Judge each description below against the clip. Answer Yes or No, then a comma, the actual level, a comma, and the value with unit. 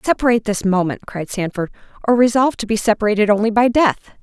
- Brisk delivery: No, average, 170 wpm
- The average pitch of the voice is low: No, high, 220 Hz